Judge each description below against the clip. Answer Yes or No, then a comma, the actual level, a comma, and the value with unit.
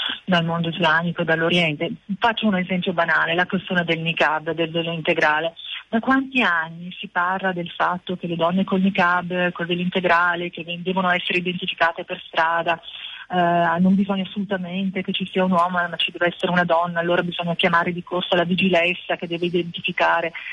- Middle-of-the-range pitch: Yes, medium, 175 Hz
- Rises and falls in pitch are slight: Yes, narrow, 1.7 semitones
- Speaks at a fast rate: Yes, fast, 185 wpm